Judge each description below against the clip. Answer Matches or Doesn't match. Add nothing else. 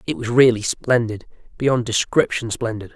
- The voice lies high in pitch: Doesn't match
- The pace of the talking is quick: Doesn't match